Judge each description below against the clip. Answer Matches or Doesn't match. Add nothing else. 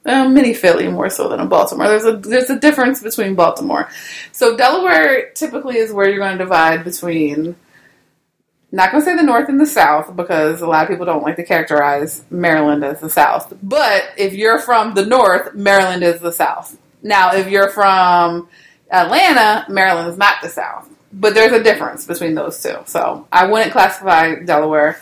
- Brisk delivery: Doesn't match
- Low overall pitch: Doesn't match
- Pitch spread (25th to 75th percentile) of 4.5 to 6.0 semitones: Matches